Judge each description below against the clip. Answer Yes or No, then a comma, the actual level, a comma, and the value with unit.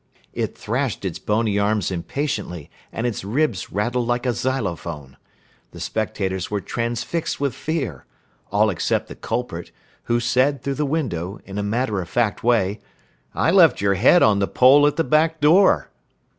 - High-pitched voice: No, low, 115 Hz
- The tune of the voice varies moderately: No, wide, 5.7 semitones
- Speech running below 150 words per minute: No, average, 165 wpm